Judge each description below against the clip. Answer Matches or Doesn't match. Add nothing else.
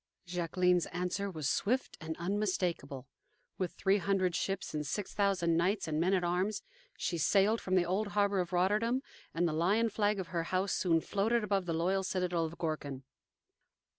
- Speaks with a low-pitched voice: Doesn't match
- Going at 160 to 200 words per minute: Matches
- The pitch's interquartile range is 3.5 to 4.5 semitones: Doesn't match